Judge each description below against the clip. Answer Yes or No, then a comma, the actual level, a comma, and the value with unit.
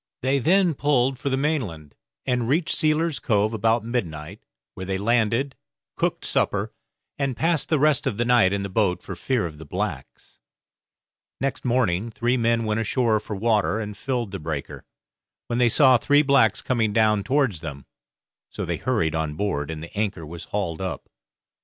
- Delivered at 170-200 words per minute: Yes, average, 180 wpm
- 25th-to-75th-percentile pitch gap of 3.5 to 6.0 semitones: Yes, wide, 5.4 semitones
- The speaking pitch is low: Yes, low, 115 Hz